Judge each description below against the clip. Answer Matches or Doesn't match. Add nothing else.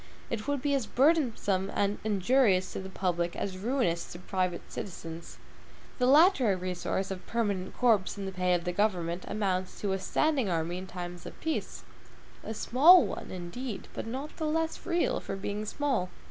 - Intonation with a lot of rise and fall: Matches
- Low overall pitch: Doesn't match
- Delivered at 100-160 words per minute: Doesn't match